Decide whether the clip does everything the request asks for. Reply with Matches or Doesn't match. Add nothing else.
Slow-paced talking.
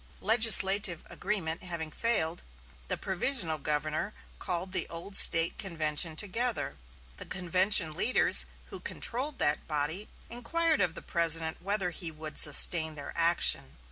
Matches